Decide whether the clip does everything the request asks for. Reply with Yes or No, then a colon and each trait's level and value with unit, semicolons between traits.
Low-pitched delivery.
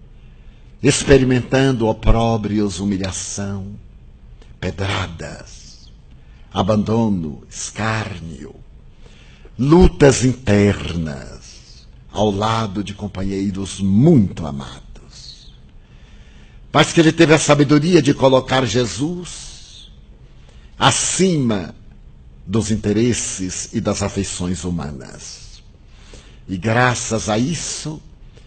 Yes: low, 105 Hz